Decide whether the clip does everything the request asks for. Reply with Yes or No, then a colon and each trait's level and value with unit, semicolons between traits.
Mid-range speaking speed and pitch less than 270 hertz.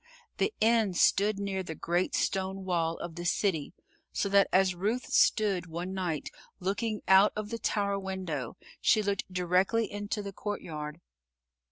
Yes: average, 155 wpm; high, 190 Hz